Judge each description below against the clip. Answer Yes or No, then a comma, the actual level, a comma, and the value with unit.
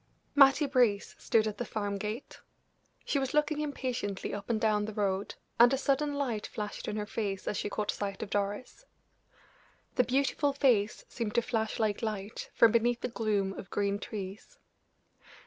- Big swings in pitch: No, average, 3.8 semitones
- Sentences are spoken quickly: No, average, 175 wpm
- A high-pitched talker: Yes, high, 220 Hz